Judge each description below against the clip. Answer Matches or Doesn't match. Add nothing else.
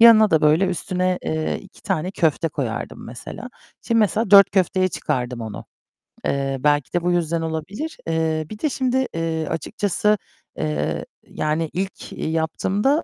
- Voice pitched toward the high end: Doesn't match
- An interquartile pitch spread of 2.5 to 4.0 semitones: Doesn't match